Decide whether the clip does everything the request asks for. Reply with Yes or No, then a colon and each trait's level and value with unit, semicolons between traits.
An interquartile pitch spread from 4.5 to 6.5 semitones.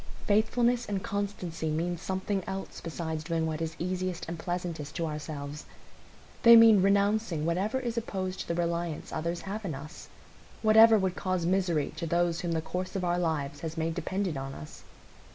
No: average, 3.4 semitones